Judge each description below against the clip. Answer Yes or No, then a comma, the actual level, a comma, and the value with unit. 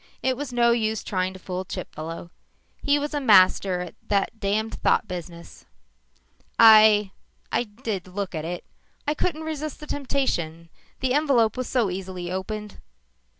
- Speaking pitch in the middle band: No, high, 210 Hz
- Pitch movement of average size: No, wide, 5.8 semitones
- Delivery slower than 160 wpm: Yes, average, 150 wpm